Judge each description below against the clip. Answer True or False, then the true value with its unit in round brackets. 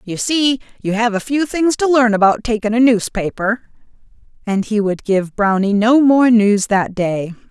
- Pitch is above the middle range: True (225 Hz)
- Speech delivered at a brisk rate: False (185 wpm)